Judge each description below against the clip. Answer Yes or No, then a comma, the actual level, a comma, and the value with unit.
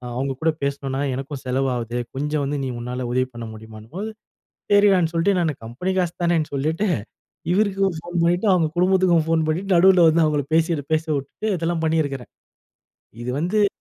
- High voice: No, medium, 160 Hz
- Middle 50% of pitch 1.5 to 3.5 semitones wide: No, average, 4.6 semitones